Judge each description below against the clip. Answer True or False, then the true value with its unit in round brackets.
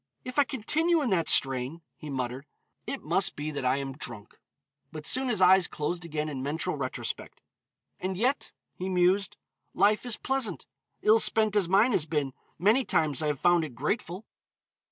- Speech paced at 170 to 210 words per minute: True (175 wpm)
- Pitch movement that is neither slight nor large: False (6.4 semitones)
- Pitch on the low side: False (175 Hz)